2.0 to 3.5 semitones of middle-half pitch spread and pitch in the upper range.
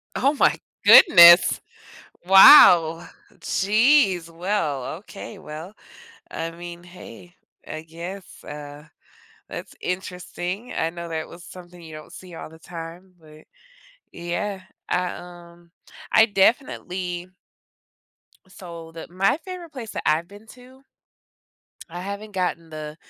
No: average, 3.0 semitones; medium, 175 Hz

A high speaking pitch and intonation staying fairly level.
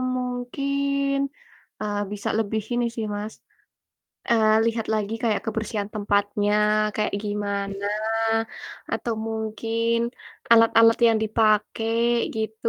Yes: high, 220 Hz; narrow, 1.7 semitones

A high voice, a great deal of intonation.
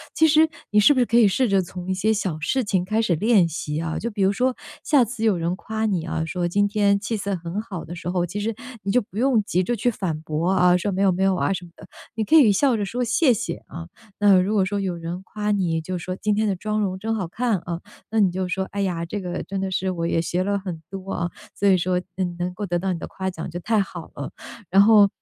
No: high, 195 Hz; average, 3.3 semitones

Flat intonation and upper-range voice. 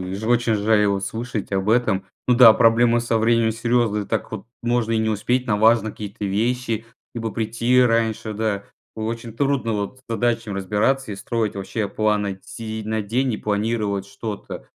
No: narrow, 2.2 semitones; low, 110 Hz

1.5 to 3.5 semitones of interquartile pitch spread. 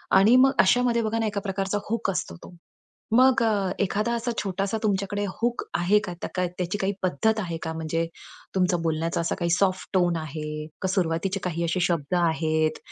No: average, 3.9 semitones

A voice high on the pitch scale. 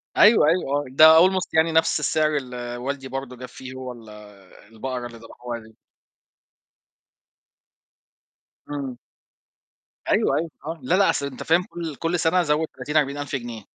No: medium, 140 Hz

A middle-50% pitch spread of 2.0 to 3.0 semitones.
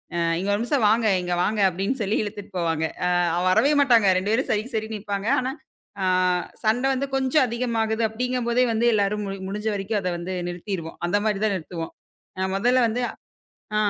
No: average, 3.4 semitones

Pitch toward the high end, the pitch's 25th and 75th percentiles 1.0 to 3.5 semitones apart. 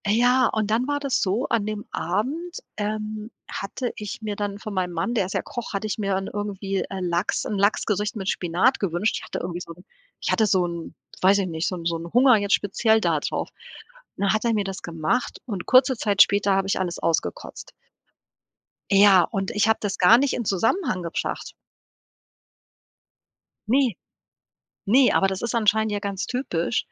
Yes: high, 205 Hz; average, 3.1 semitones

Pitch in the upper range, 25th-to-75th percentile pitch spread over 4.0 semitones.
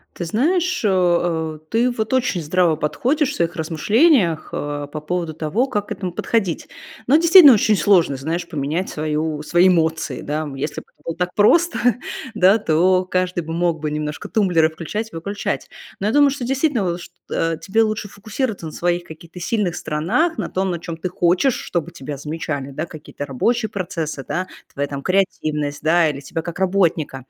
No: medium, 175 Hz; average, 4.9 semitones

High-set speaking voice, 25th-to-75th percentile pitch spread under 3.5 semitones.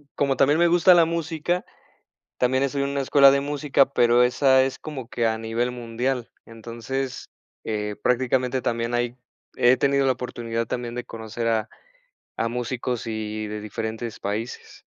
No: low, 125 Hz; average, 3.1 semitones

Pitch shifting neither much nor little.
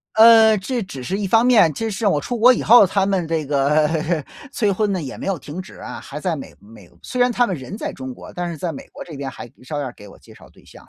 No: wide, 6.8 semitones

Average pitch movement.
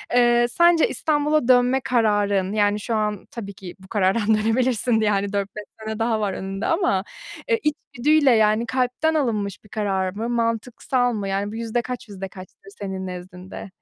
Yes: average, 3.6 semitones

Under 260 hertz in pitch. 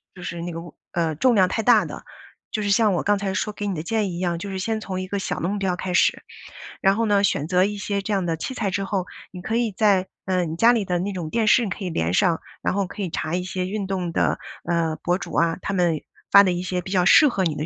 Yes: medium, 185 Hz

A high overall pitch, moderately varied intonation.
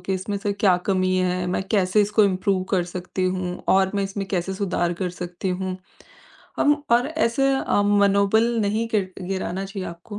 No: high, 195 Hz; narrow, 1.8 semitones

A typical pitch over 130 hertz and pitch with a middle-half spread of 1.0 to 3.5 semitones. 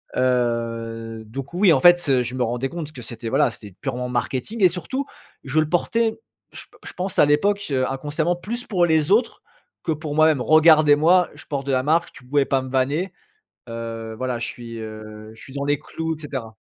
No: medium, 140 Hz; average, 5.2 semitones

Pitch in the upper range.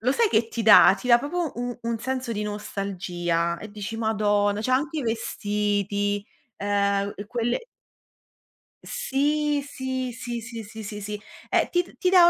Yes: high, 225 Hz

